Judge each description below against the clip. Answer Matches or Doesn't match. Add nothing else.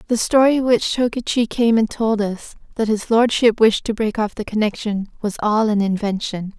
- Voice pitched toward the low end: Doesn't match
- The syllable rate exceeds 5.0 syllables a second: Doesn't match